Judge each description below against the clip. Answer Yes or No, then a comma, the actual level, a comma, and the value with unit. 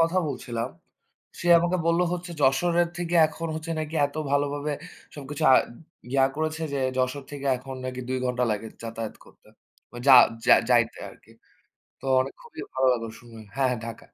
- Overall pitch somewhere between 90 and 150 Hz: Yes, medium, 140 Hz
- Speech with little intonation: No, average, 4.2 semitones